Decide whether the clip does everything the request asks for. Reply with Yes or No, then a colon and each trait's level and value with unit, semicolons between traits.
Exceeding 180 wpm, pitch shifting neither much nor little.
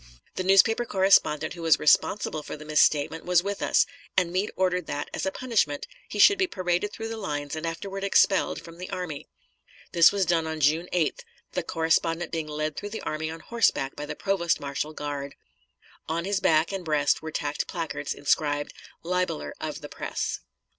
Yes: average, 190 wpm; average, 3.8 semitones